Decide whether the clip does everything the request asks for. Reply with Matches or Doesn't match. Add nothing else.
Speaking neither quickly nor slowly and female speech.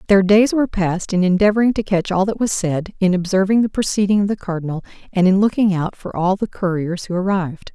Doesn't match